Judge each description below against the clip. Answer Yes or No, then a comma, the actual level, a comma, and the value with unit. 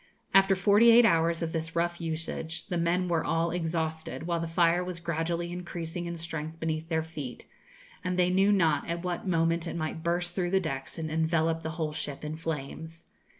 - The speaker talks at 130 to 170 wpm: No, average, 195 wpm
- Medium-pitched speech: Yes, medium, 165 Hz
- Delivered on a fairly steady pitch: Yes, narrow, 1.4 semitones